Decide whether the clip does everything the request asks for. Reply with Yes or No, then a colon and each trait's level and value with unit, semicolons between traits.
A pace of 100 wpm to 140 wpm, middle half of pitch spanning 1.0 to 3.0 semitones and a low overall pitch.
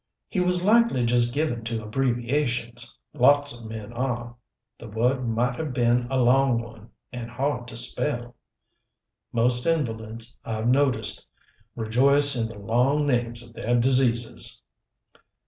Yes: slow, 135 wpm; narrow, 2.5 semitones; low, 120 Hz